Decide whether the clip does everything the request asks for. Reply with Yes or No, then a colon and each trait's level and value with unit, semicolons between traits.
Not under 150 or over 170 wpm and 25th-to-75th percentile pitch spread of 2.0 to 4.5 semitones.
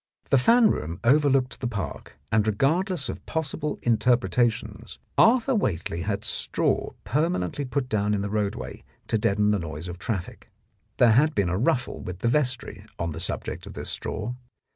No: average, 165 wpm; wide, 5.4 semitones